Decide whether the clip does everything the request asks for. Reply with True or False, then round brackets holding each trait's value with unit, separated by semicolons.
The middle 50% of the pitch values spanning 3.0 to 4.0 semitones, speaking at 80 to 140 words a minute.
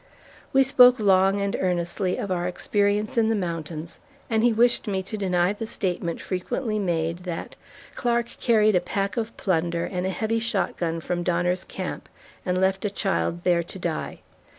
False (3.6 semitones; 175 wpm)